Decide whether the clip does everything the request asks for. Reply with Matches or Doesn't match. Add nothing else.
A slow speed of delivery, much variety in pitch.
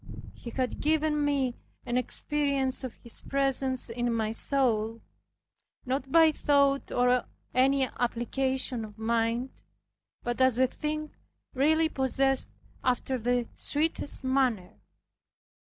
Doesn't match